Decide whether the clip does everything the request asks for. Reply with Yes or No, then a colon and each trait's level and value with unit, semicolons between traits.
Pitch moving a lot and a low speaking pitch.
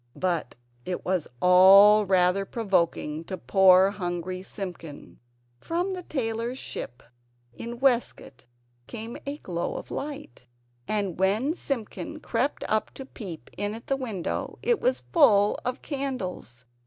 No: wide, 6.1 semitones; high, 205 Hz